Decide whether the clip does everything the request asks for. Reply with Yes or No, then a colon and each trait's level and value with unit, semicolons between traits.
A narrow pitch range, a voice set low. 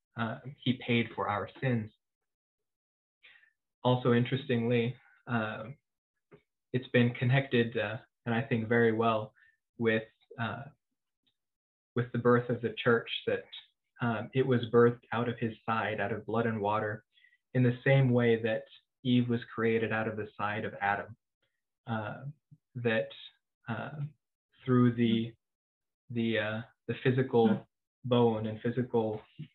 Yes: narrow, 2.0 semitones; low, 120 Hz